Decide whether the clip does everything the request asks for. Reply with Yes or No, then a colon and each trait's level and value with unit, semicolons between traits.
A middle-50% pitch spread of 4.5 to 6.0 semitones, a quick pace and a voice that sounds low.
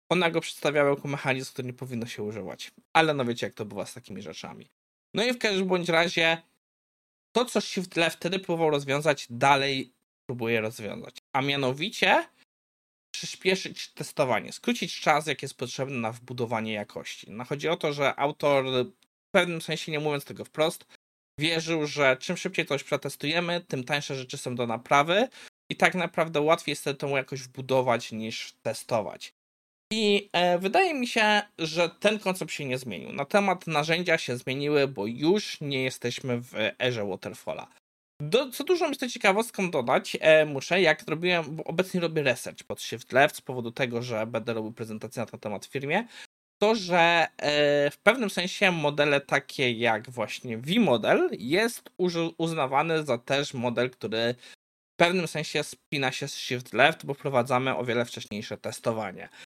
No: wide, 5.4 semitones; fast, 165 wpm; medium, 145 Hz